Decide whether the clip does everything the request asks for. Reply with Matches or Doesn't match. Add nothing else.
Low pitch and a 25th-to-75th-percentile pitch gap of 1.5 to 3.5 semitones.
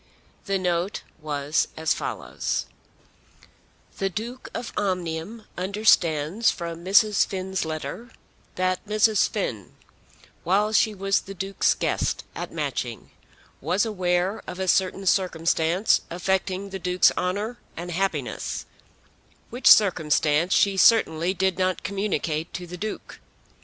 Doesn't match